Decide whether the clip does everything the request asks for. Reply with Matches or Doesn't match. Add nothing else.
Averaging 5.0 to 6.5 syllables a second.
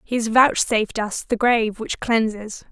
Doesn't match